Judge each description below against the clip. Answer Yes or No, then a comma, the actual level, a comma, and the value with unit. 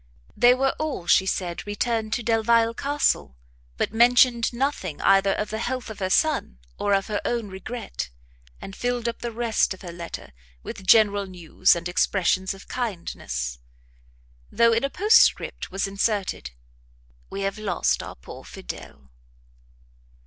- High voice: Yes, high, 210 Hz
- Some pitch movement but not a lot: Yes, average, 4.1 semitones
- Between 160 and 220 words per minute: No, average, 150 wpm